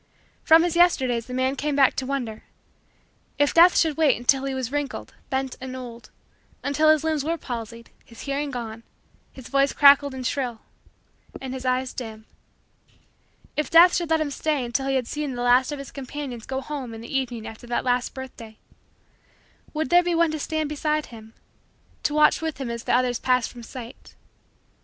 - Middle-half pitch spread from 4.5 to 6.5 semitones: No, average, 3.5 semitones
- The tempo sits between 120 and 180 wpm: No, average, 190 wpm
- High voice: Yes, very high, 265 Hz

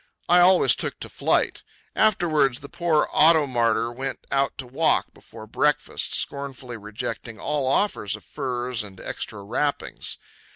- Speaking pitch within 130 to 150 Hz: Yes, low, 135 Hz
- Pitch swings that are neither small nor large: Yes, average, 4.3 semitones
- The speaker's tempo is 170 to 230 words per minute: No, average, 140 wpm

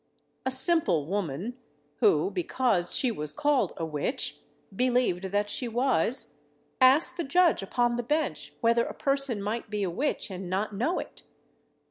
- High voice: Yes, high, 230 Hz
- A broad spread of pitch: Yes, wide, 5.9 semitones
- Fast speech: No, average, 155 wpm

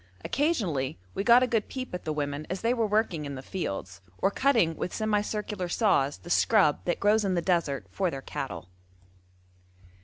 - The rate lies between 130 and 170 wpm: No, average, 190 wpm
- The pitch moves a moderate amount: No, wide, 6.8 semitones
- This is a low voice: No, medium, 185 Hz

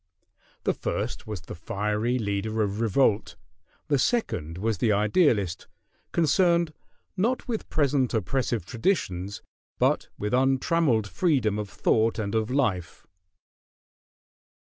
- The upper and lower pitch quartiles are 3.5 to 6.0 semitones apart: Yes, wide, 5.6 semitones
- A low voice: Yes, low, 110 Hz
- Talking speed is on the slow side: Yes, slow, 115 wpm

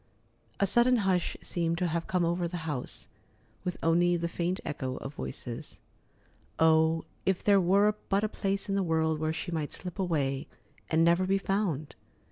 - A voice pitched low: No, medium, 170 Hz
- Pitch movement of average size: Yes, average, 3.1 semitones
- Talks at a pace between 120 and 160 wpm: No, average, 175 wpm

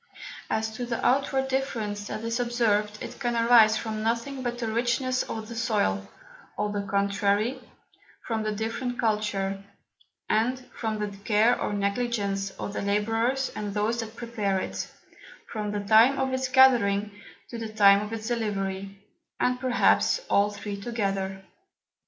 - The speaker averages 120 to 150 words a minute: No, average, 160 wpm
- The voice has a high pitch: Yes, high, 220 Hz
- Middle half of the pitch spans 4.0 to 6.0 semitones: No, average, 2.8 semitones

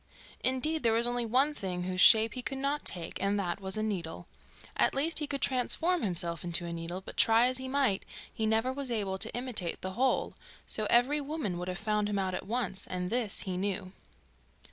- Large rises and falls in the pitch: Yes, wide, 5.7 semitones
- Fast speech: Yes, fast, 215 wpm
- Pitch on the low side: No, high, 220 Hz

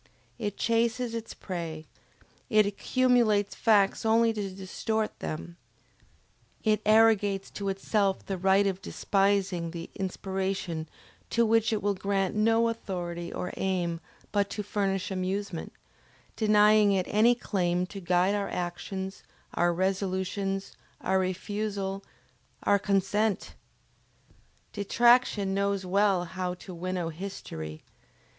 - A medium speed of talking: No, slow, 115 wpm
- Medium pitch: No, high, 195 Hz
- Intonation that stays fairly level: Yes, narrow, 2.3 semitones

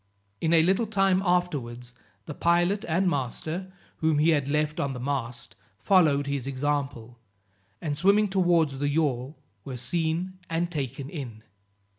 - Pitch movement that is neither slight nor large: Yes, average, 4.5 semitones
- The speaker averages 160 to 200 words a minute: No, average, 145 wpm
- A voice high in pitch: No, medium, 150 Hz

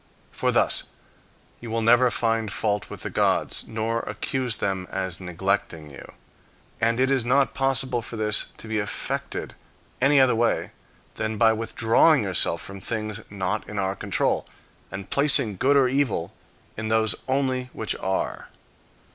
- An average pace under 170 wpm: Yes, average, 155 wpm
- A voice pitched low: Yes, low, 110 Hz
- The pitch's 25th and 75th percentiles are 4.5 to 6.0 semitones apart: No, average, 3.7 semitones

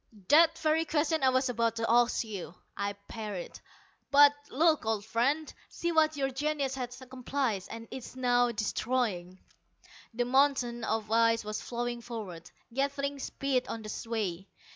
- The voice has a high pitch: Yes, high, 245 Hz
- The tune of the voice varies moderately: Yes, average, 3.9 semitones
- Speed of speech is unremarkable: Yes, average, 150 wpm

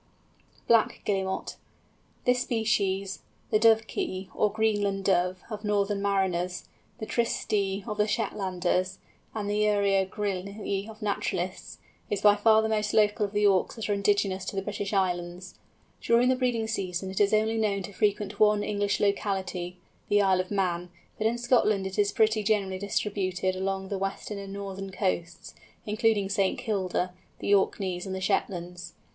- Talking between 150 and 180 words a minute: Yes, average, 160 wpm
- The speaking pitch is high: Yes, high, 200 Hz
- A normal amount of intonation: No, narrow, 1.9 semitones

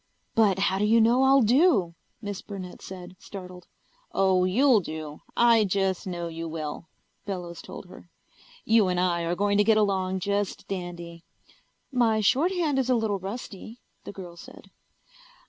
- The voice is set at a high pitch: Yes, high, 195 Hz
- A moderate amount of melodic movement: Yes, average, 3.9 semitones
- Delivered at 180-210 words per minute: No, average, 160 wpm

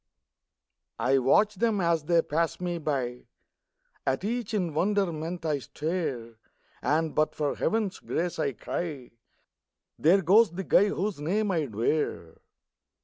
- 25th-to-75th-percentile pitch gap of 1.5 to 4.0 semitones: No, average, 4.8 semitones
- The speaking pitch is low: No, medium, 165 Hz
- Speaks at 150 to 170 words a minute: No, slow, 135 wpm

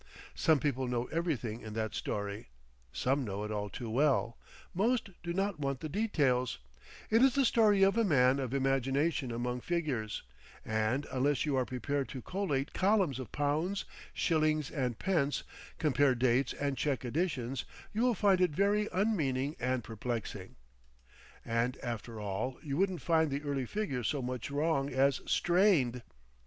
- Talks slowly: No, average, 160 wpm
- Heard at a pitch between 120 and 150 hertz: Yes, medium, 140 Hz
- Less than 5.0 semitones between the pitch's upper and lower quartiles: No, wide, 5.5 semitones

